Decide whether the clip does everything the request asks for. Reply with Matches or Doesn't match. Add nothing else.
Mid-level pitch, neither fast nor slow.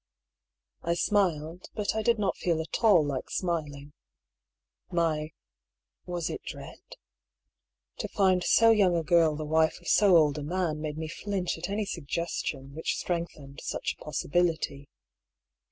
Matches